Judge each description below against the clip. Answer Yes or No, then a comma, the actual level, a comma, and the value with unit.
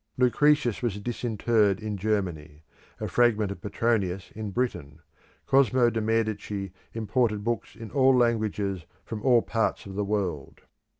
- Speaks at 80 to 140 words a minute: Yes, slow, 135 wpm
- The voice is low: Yes, low, 110 Hz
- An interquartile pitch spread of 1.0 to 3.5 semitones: Yes, average, 3.2 semitones